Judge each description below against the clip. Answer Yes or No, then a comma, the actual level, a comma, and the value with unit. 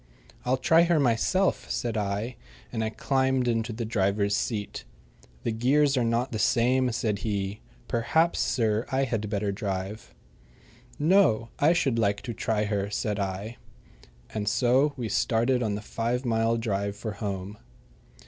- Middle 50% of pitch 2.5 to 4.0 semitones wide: Yes, average, 3.5 semitones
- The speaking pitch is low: Yes, low, 115 Hz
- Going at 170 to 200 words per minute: No, average, 155 wpm